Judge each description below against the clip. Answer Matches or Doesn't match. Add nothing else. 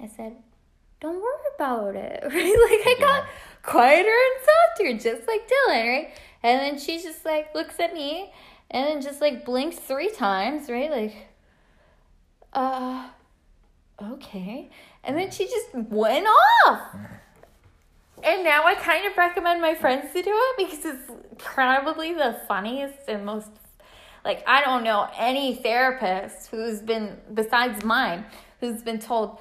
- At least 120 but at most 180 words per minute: Matches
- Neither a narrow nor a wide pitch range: Doesn't match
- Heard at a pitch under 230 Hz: Doesn't match